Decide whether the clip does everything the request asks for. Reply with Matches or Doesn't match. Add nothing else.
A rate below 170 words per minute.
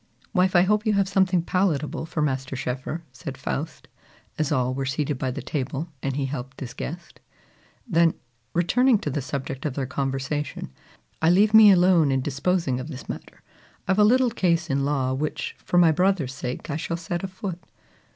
Doesn't match